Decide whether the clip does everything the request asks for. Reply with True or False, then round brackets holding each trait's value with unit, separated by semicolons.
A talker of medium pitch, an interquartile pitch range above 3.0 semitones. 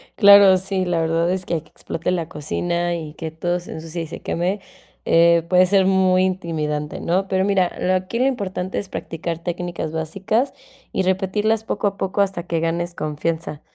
False (180 Hz; 2.4 semitones)